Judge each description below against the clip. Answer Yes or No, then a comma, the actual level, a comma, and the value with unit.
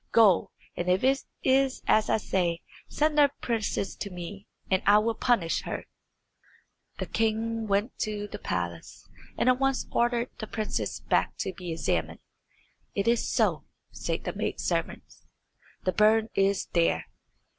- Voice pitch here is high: Yes, high, 215 Hz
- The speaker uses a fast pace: No, average, 155 wpm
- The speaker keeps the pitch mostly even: No, average, 3.8 semitones